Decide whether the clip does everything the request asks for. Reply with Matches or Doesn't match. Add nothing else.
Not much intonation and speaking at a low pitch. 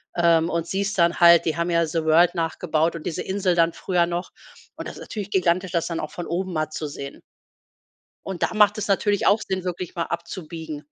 Doesn't match